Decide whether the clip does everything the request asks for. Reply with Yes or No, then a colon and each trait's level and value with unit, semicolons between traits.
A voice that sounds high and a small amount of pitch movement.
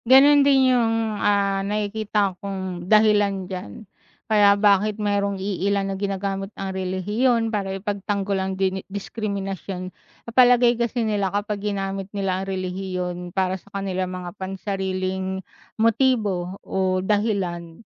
Yes: high, 195 Hz; narrow, 2.0 semitones